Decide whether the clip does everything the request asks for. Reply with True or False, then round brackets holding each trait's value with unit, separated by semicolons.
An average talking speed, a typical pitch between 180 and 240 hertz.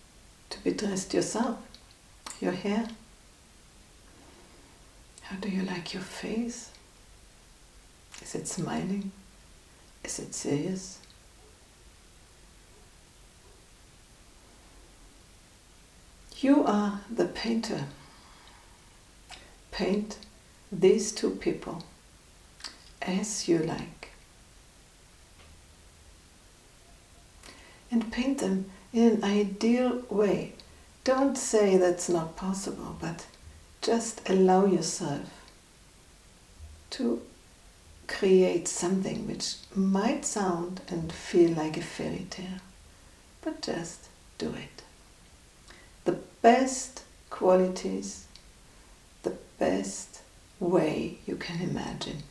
False (80 wpm; 185 Hz)